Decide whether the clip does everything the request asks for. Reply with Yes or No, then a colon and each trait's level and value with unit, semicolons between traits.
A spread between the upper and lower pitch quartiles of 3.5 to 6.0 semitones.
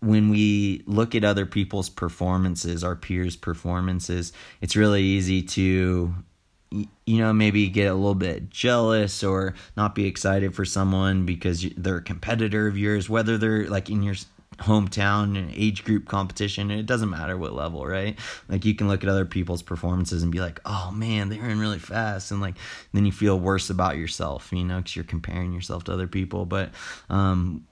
No: narrow, 2.4 semitones